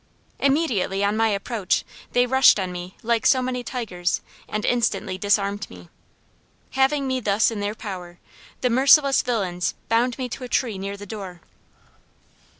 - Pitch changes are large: No, average, 4.3 semitones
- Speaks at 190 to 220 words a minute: No, average, 155 wpm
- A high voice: Yes, high, 215 Hz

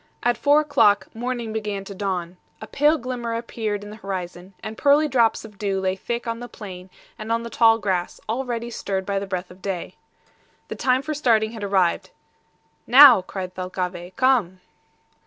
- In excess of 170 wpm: Yes, average, 180 wpm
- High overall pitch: Yes, high, 215 Hz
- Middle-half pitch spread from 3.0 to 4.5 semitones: Yes, average, 3.9 semitones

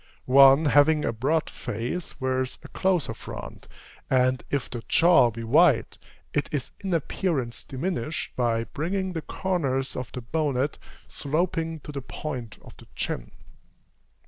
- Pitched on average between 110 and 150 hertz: Yes, medium, 140 Hz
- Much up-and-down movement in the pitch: No, average, 4.3 semitones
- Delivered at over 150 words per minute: No, average, 145 wpm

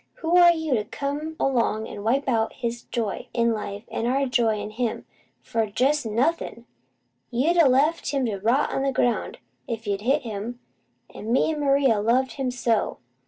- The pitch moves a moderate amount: Yes, average, 3.8 semitones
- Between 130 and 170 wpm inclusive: No, average, 190 wpm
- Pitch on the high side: Yes, high, 245 Hz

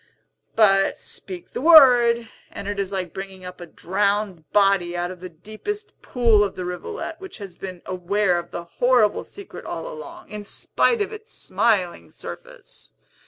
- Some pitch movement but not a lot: No, wide, 6.7 semitones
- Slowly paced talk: No, average, 165 wpm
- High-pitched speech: Yes, high, 205 Hz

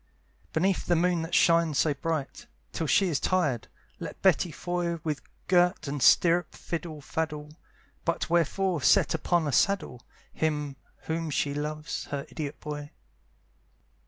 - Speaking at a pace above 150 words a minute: No, average, 140 wpm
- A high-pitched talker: No, medium, 160 Hz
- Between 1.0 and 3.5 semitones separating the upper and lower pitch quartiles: Yes, average, 2.8 semitones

